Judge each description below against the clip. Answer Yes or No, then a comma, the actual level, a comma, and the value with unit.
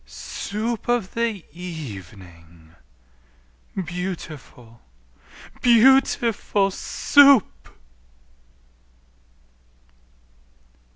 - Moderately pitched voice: Yes, medium, 180 Hz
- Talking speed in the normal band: No, slow, 60 wpm